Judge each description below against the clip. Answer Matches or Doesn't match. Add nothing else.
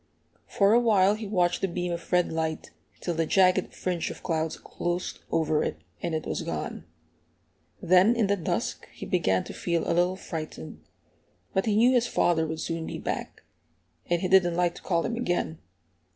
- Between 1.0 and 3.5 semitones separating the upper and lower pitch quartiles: Matches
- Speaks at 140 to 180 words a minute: Doesn't match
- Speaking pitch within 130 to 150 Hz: Doesn't match